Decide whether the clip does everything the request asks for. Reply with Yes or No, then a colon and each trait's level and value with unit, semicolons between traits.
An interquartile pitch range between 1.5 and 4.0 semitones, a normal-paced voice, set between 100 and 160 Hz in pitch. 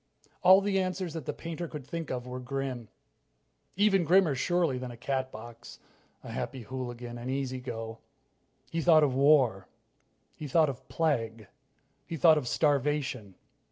No: average, 4.9 semitones; average, 155 wpm; low, 135 Hz